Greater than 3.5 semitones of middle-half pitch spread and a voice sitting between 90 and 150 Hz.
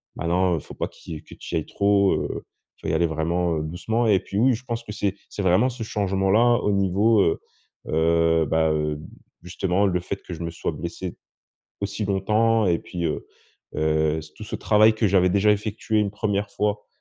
Yes: average, 4.1 semitones; very low, 95 Hz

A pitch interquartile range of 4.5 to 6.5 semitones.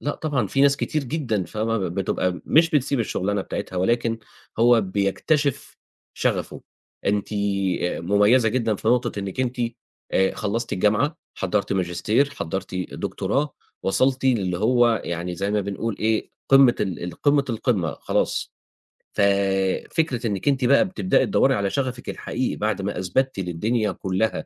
Yes: average, 5.1 semitones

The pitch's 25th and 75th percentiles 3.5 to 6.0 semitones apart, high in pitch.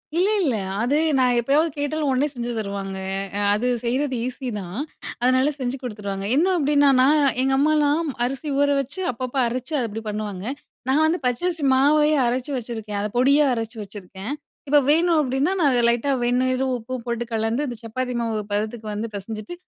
Yes: average, 4.2 semitones; very high, 255 Hz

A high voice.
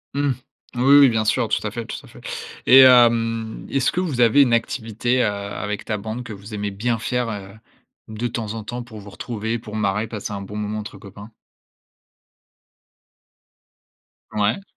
No: low, 110 Hz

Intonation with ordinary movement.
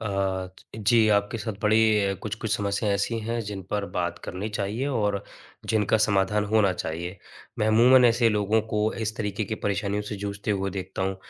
No: narrow, 1.9 semitones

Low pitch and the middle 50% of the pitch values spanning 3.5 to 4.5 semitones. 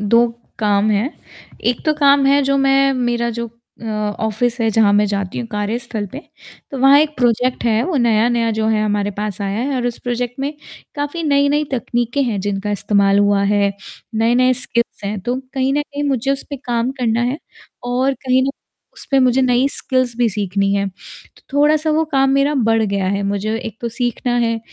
No: high, 240 Hz; average, 4.2 semitones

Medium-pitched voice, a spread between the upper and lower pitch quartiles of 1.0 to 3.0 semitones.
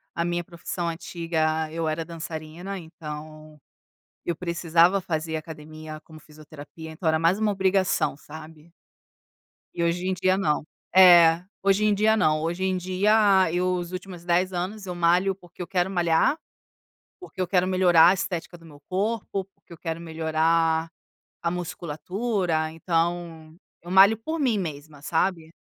Yes: medium, 170 Hz; narrow, 2.6 semitones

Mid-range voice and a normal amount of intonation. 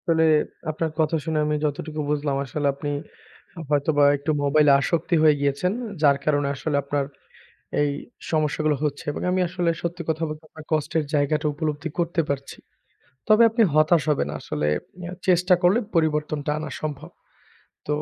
No: medium, 155 Hz; narrow, 2.2 semitones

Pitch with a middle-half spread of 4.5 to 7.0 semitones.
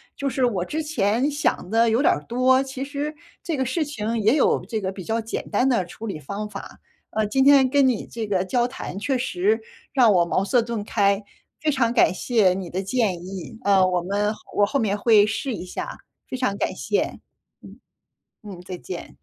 Yes: average, 5.0 semitones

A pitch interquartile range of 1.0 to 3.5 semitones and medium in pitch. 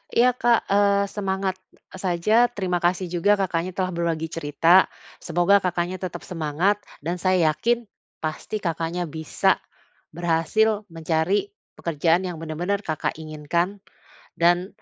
Yes: average, 3.1 semitones; medium, 175 Hz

